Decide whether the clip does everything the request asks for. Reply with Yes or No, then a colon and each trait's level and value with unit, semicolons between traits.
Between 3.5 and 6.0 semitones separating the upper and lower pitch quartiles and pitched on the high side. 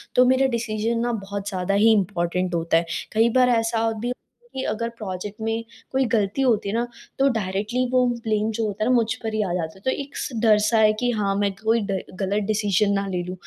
No: average, 2.9 semitones; high, 215 Hz